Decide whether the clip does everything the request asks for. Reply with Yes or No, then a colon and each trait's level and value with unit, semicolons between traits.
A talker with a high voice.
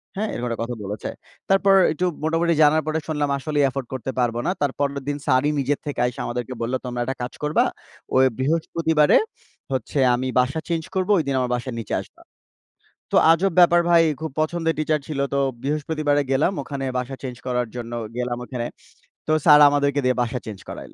No: medium, 140 Hz